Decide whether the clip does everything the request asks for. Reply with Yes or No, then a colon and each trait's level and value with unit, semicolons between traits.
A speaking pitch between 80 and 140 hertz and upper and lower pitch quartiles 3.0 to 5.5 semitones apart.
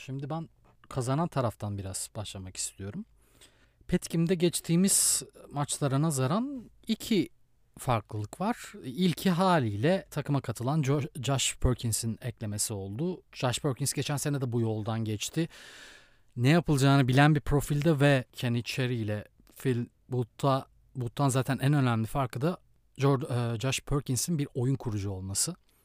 Yes: low, 135 Hz; average, 4.3 semitones